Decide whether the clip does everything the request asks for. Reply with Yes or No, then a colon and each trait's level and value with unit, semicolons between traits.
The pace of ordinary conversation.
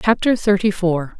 Yes: average, 150 wpm